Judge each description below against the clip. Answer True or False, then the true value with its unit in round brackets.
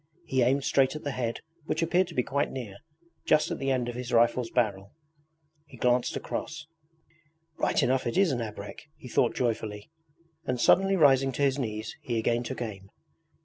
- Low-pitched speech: True (125 Hz)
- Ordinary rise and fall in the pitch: True (3.0 semitones)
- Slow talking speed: False (190 wpm)